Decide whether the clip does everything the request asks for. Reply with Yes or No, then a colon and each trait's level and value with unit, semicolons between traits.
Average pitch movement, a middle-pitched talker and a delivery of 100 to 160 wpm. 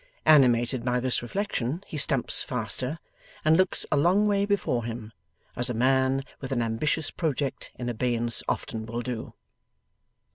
No: average, 4.3 semitones; low, 125 Hz; average, 150 wpm